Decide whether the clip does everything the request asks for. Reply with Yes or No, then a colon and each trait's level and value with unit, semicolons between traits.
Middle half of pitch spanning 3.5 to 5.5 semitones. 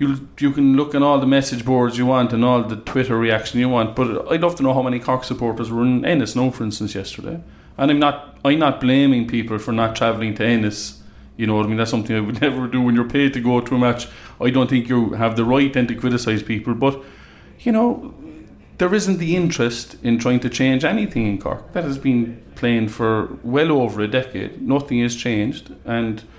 No: average, 3.1 semitones